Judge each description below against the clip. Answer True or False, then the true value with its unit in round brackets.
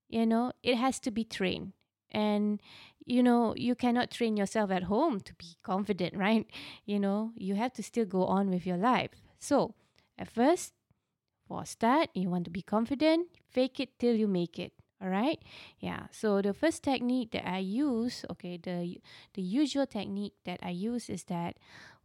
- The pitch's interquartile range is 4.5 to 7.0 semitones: True (4.8 semitones)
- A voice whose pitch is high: True (215 Hz)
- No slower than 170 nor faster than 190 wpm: True (185 wpm)